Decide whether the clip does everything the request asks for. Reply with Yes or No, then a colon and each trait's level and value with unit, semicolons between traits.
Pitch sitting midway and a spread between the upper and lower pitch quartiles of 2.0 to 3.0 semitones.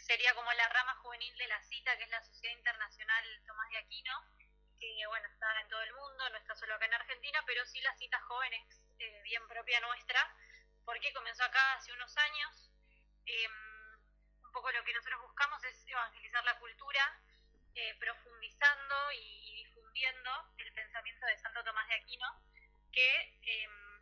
No: high, 240 Hz; narrow, 2.5 semitones